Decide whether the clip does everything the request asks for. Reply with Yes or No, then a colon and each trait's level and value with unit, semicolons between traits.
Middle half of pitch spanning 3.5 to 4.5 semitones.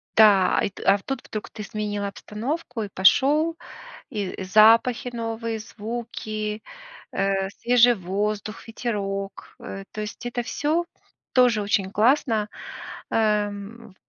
No: average, 2.7 semitones